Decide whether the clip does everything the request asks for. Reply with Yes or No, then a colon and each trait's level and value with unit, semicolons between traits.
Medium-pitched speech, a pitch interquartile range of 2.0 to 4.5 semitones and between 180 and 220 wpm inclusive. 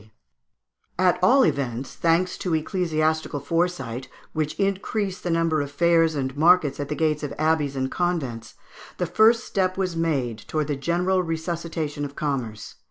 No: medium, 160 Hz; average, 3.8 semitones; average, 160 wpm